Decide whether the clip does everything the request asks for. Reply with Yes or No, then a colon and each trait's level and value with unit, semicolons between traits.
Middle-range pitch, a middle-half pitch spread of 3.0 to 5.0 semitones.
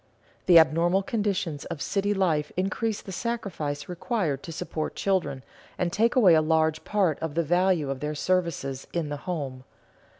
Yes: medium, 170 Hz; average, 4.1 semitones